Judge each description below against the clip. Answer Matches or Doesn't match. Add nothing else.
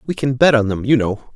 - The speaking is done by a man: Matches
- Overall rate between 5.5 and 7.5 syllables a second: Matches